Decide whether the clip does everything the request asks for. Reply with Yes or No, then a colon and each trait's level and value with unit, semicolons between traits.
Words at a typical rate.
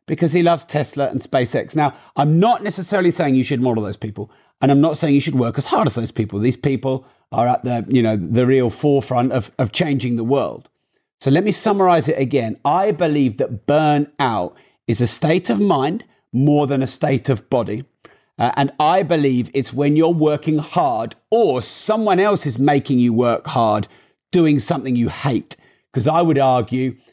Yes: average, 195 wpm